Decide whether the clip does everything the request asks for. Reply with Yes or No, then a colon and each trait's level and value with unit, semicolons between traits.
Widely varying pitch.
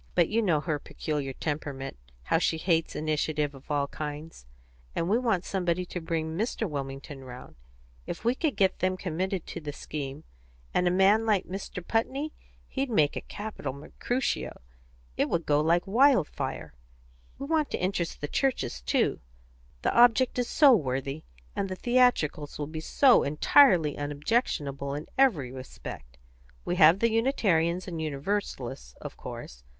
Yes: wide, 6.5 semitones